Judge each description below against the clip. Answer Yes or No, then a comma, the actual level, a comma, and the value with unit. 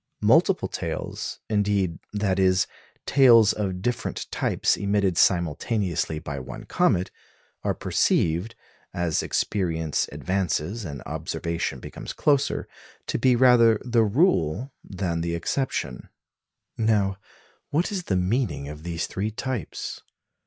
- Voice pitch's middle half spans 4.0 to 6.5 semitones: Yes, wide, 5.4 semitones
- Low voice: Yes, very low, 95 Hz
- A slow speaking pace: Yes, slow, 115 wpm